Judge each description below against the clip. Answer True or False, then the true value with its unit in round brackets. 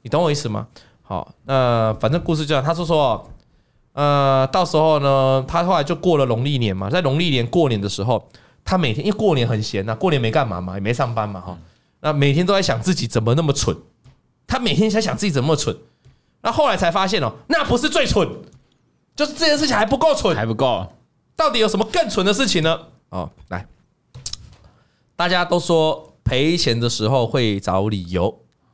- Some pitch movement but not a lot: False (7.1 semitones)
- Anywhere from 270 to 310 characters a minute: True (290 characters per minute)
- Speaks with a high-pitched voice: False (140 Hz)